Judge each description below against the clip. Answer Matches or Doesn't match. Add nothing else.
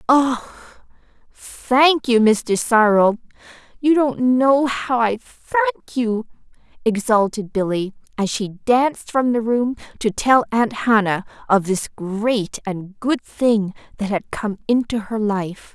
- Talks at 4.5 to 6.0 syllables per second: Doesn't match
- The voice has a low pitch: Doesn't match